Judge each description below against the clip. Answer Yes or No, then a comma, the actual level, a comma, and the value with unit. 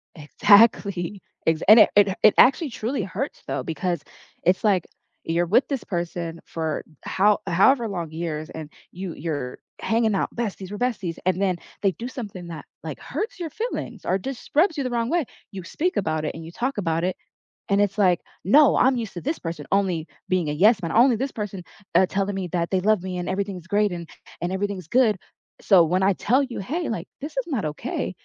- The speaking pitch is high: Yes, high, 195 Hz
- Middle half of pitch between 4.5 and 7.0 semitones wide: Yes, average, 5.1 semitones